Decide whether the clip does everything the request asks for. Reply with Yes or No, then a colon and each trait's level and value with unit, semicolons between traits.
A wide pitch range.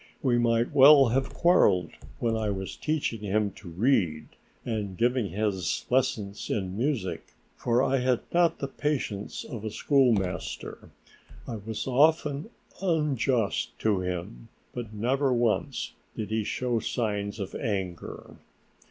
No: average, 4.7 semitones